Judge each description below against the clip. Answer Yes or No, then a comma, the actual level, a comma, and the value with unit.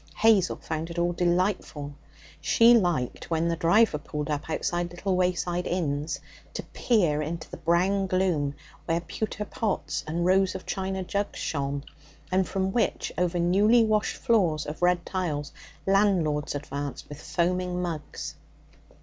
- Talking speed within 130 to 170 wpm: Yes, average, 145 wpm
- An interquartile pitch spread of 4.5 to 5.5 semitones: No, average, 3.3 semitones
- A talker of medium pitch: Yes, medium, 175 Hz